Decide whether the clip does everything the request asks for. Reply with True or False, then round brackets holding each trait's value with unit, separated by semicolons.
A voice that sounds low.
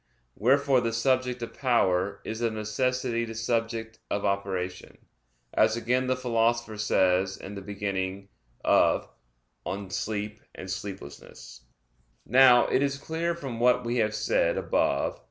True (115 Hz)